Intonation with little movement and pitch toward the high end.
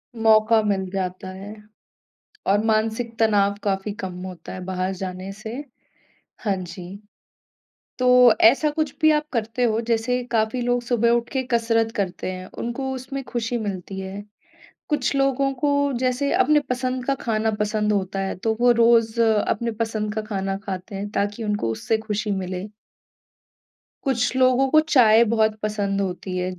No: average, 3.8 semitones; high, 220 Hz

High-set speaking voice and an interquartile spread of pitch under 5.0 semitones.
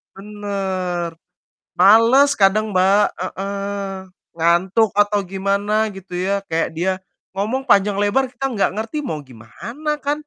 Yes: high, 200 Hz; narrow, 2.6 semitones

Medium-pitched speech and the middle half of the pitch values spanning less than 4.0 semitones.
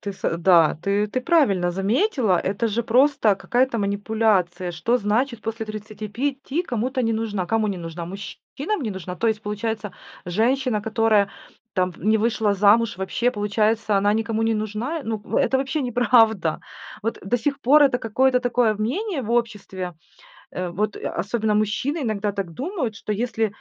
No: high, 220 Hz; average, 3.5 semitones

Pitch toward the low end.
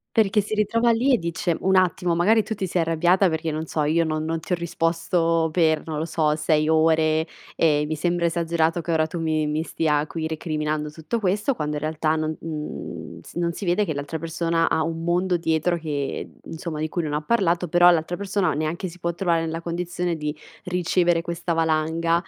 No: medium, 165 Hz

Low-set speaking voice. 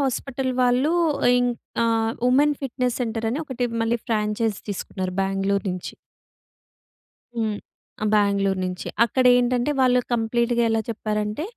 No: high, 230 Hz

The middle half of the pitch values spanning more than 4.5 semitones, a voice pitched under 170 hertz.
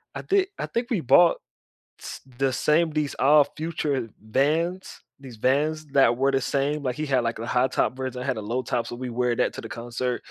No: average, 3.6 semitones; low, 135 Hz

